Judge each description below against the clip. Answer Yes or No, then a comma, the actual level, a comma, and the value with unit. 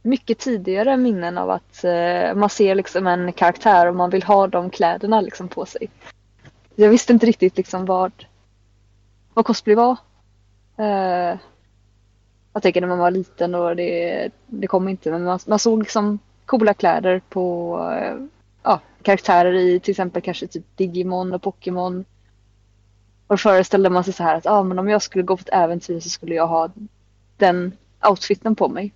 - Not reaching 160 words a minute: No, average, 175 wpm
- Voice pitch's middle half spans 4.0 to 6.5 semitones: No, average, 3.5 semitones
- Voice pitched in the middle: Yes, medium, 180 Hz